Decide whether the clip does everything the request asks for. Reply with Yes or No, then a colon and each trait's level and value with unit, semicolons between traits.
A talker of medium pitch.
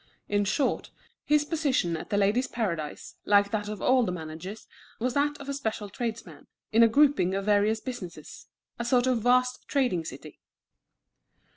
No: high, 220 Hz